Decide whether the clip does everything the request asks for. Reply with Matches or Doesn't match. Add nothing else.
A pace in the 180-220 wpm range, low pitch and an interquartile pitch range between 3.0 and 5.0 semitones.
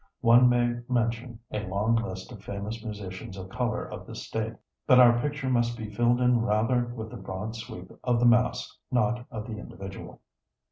Doesn't match